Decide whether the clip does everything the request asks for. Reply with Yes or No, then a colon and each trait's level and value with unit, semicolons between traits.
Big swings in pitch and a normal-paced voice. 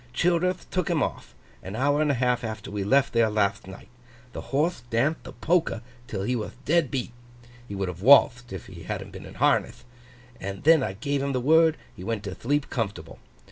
No: wide, 5.9 semitones; fast, 215 wpm